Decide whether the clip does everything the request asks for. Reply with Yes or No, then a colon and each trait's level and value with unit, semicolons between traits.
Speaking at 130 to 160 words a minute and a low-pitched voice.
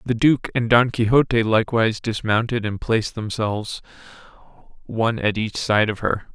Yes: average, 150 wpm; low, 110 Hz